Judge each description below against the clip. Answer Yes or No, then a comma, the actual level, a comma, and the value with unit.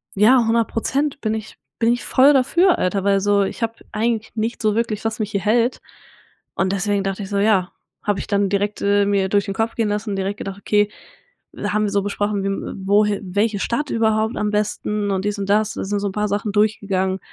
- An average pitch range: No, narrow, 1.8 semitones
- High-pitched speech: Yes, high, 210 Hz